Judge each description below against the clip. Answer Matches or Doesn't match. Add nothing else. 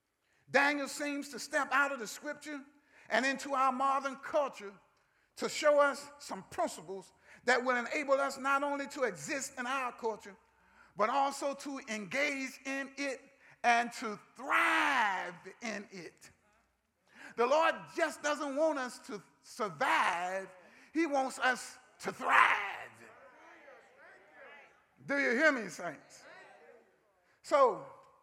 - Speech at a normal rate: Doesn't match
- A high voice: Matches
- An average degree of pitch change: Matches